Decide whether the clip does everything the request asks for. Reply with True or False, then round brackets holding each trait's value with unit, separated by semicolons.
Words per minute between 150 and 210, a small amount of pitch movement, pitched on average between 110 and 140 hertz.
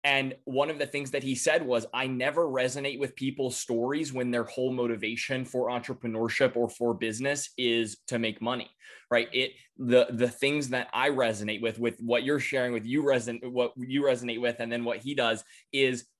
True (200 wpm; 2.3 semitones; 125 Hz)